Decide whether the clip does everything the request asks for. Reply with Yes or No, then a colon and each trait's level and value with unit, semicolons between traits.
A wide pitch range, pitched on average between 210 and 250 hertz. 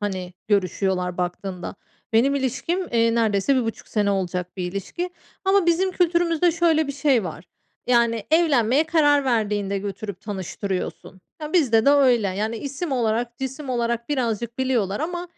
Yes: wide, 6.4 semitones; high, 235 Hz